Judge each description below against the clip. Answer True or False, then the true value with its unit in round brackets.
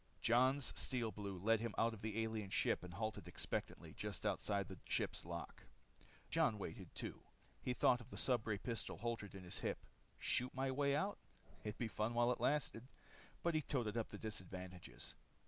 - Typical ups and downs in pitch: True (3.5 semitones)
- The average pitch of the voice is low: True (110 Hz)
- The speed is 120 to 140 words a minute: False (185 wpm)